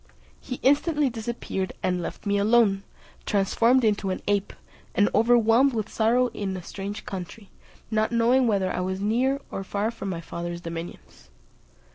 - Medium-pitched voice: No, high, 210 Hz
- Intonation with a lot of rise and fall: No, average, 3.7 semitones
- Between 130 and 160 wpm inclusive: Yes, average, 155 wpm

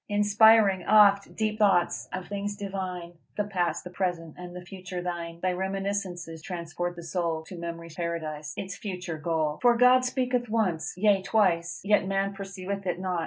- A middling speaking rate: Yes, average, 165 wpm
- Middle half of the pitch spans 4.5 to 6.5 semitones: No, average, 3.0 semitones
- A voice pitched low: No, medium, 185 Hz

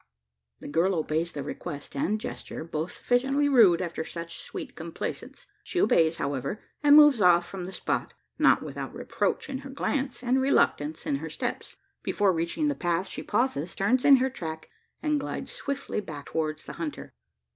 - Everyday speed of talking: Yes, average, 175 wpm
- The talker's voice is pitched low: No, medium, 185 Hz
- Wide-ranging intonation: Yes, wide, 8.6 semitones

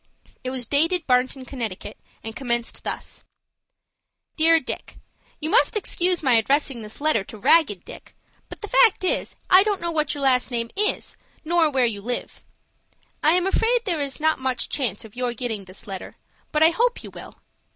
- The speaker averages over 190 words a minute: No, average, 180 wpm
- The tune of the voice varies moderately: No, wide, 6.1 semitones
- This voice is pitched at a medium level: No, very high, 280 Hz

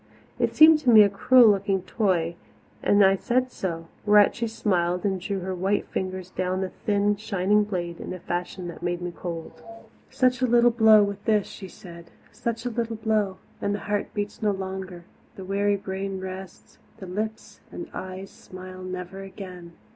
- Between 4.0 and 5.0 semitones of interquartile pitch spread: No, narrow, 2.5 semitones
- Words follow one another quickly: No, average, 185 wpm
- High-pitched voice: Yes, high, 195 Hz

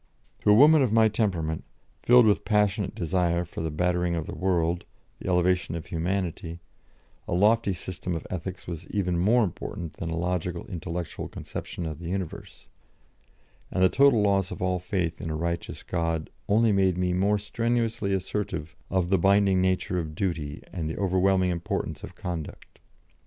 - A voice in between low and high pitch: No, very low, 90 Hz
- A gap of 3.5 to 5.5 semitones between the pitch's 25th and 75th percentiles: No, average, 2.8 semitones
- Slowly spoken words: No, average, 175 wpm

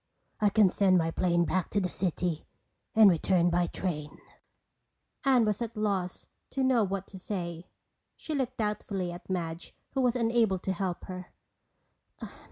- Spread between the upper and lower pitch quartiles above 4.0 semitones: No, average, 3.7 semitones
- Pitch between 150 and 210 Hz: Yes, high, 190 Hz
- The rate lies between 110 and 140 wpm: No, average, 165 wpm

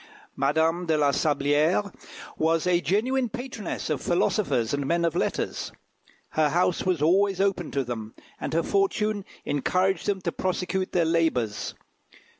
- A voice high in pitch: No, medium, 170 Hz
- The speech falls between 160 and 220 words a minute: No, average, 145 wpm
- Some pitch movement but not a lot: Yes, average, 4.4 semitones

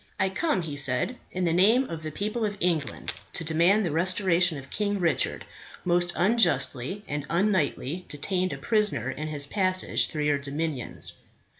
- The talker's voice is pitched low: No, medium, 175 Hz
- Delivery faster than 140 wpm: Yes, average, 165 wpm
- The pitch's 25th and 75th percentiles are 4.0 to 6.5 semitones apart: Yes, average, 4.9 semitones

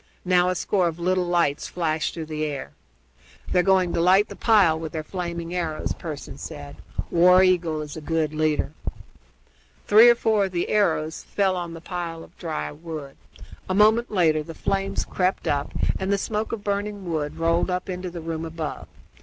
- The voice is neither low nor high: Yes, medium, 170 Hz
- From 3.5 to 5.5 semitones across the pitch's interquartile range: No, average, 3.0 semitones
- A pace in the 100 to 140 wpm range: No, average, 185 wpm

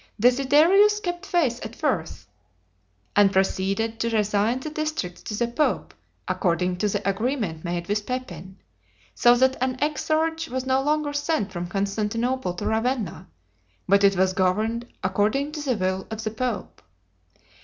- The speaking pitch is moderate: No, high, 225 Hz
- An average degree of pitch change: No, wide, 5.7 semitones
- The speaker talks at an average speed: Yes, average, 150 wpm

